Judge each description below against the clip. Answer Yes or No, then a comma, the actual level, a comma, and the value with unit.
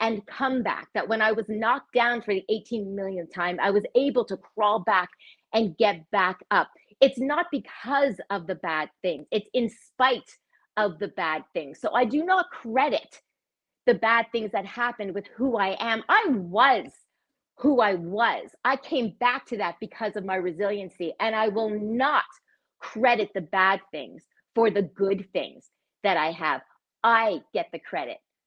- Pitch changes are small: No, average, 3.9 semitones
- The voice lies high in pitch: Yes, high, 220 Hz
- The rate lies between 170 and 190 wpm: Yes, average, 180 wpm